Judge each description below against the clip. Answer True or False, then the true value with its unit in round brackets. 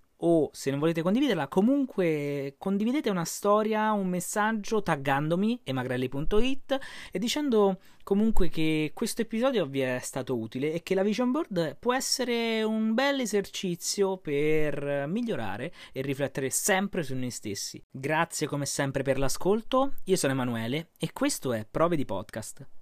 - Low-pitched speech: False (175 Hz)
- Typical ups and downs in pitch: False (7.6 semitones)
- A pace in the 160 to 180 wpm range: False (145 wpm)